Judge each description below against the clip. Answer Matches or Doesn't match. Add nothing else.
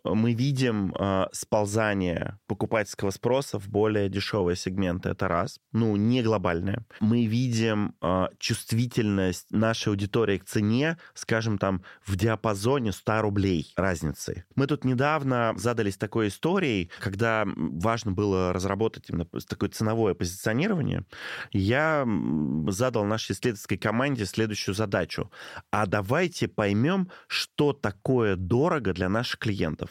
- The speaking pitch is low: Matches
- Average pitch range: Matches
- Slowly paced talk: Doesn't match